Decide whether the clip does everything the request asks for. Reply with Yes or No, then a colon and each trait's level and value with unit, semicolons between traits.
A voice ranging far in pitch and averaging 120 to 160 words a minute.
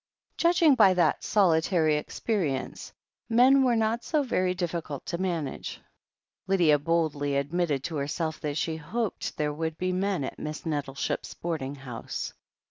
No: average, 4.4 semitones; average, 140 wpm